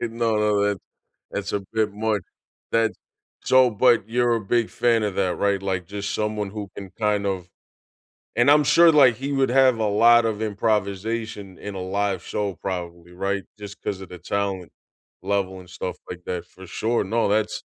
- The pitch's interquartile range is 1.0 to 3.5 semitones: Yes, average, 2.8 semitones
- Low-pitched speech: Yes, low, 105 Hz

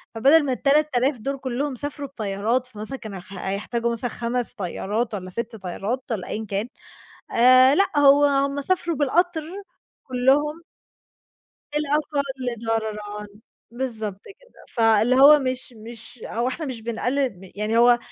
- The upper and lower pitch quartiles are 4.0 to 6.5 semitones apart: Yes, average, 4.3 semitones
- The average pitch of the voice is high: Yes, high, 245 Hz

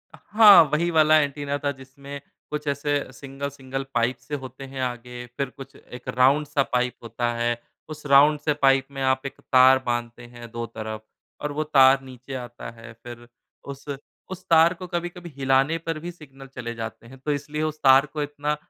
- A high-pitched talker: No, low, 135 Hz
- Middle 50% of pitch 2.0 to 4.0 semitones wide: Yes, average, 3.1 semitones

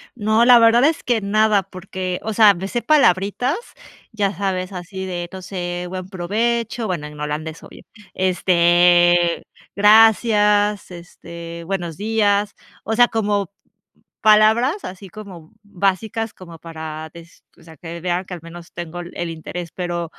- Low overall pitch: No, medium, 185 Hz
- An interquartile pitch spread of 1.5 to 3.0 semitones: No, average, 3.7 semitones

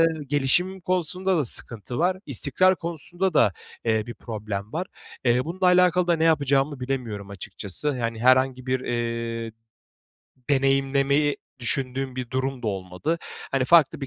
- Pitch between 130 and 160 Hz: Yes, low, 135 Hz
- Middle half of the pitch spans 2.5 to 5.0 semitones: No, wide, 5.6 semitones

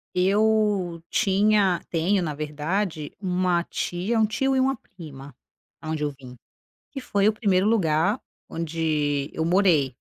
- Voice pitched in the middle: Yes, medium, 180 Hz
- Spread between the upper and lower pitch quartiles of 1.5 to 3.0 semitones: No, average, 5.0 semitones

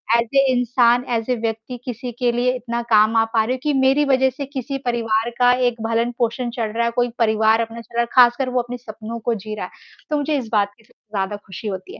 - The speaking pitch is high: Yes, high, 235 Hz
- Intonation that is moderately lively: No, narrow, 1.9 semitones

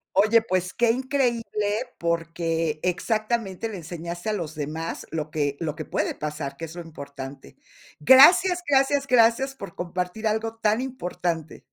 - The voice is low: No, medium, 180 Hz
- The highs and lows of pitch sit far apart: Yes, wide, 6.1 semitones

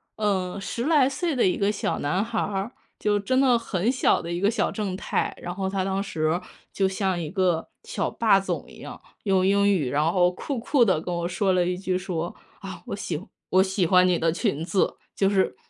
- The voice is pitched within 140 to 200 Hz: Yes, high, 190 Hz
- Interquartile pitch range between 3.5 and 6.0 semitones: No, narrow, 2.6 semitones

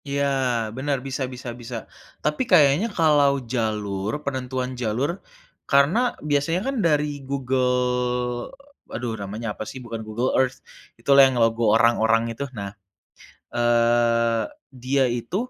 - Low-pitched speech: Yes, low, 125 Hz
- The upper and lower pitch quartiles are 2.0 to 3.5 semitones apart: Yes, average, 3.1 semitones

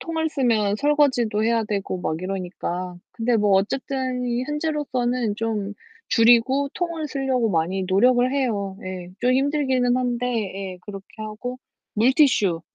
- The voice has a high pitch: Yes, high, 235 Hz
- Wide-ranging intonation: No, average, 4.8 semitones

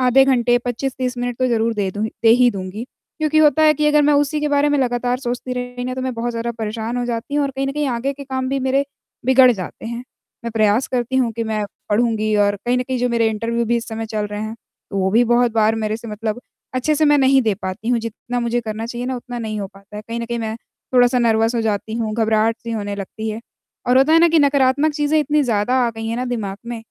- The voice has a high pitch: Yes, high, 240 Hz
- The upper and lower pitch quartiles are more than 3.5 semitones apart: No, average, 2.8 semitones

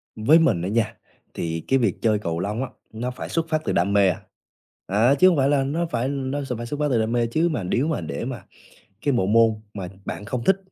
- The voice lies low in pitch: Yes, low, 120 Hz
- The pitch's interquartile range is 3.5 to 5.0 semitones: No, wide, 5.5 semitones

